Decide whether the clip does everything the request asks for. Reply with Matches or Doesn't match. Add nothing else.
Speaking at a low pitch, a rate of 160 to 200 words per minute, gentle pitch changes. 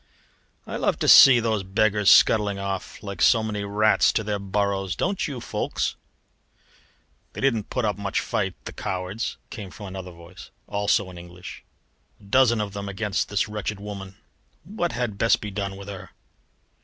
Matches